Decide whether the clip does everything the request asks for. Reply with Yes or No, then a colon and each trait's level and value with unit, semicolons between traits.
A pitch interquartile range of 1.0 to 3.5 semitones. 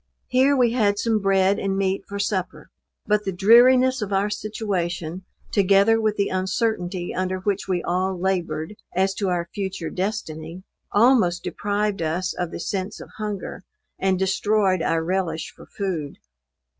Yes: narrow, 2.5 semitones